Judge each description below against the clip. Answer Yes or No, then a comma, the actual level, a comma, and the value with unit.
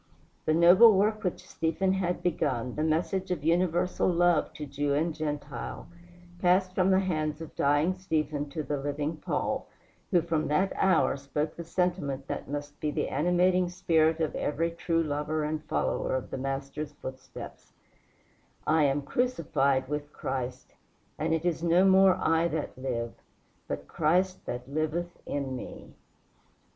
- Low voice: No, medium, 155 Hz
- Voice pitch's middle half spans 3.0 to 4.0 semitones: Yes, average, 3.4 semitones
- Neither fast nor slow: Yes, average, 155 wpm